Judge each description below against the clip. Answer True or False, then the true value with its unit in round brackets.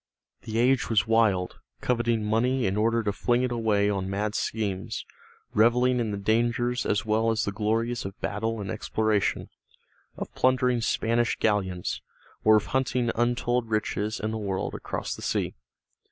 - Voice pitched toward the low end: True (110 Hz)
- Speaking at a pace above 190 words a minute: False (160 wpm)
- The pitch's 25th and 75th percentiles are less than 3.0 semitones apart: True (2.4 semitones)